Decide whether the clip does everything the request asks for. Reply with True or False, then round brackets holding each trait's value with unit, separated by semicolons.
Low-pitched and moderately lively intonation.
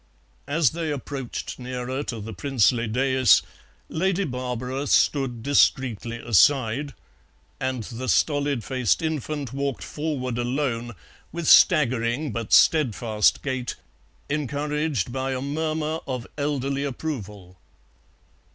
True (130 Hz; 3.5 semitones)